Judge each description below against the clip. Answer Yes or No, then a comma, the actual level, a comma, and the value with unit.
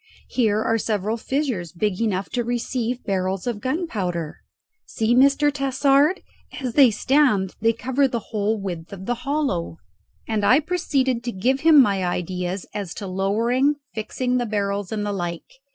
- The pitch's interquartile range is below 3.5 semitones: No, average, 5.1 semitones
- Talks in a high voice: Yes, high, 225 Hz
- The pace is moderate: Yes, average, 160 wpm